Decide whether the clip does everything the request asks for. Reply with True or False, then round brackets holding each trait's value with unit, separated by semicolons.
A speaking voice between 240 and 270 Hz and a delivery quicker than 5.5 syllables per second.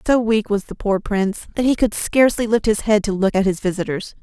False (210 Hz; 5.9 syllables/s)